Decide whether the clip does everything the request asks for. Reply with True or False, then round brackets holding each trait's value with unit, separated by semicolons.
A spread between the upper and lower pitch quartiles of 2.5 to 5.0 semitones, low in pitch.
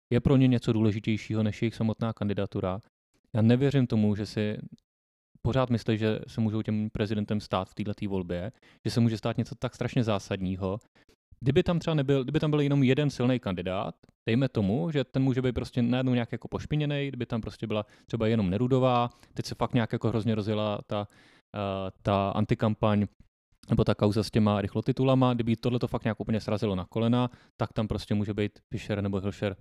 True (2.9 semitones; 110 Hz)